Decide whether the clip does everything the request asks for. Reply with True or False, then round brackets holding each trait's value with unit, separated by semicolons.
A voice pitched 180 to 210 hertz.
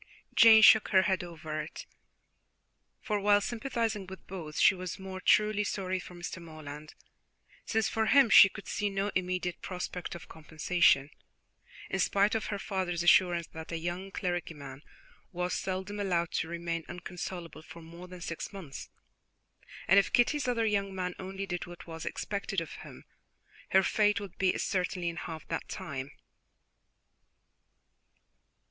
True (185 Hz)